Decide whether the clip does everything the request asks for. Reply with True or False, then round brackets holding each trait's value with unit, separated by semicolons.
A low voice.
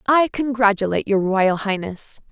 False (215 Hz)